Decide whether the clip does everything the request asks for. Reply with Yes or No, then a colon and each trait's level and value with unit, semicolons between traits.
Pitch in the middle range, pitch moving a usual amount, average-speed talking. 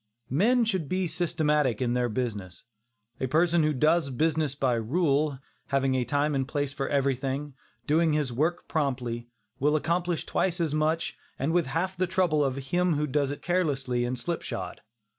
Yes: medium, 150 Hz; average, 3.9 semitones; average, 170 wpm